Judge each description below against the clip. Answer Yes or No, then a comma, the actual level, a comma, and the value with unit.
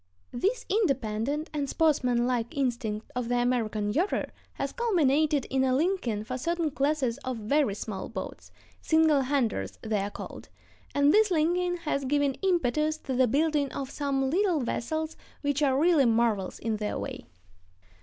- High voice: Yes, very high, 275 Hz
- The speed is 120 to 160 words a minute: Yes, average, 145 wpm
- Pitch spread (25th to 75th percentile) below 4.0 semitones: No, average, 4.7 semitones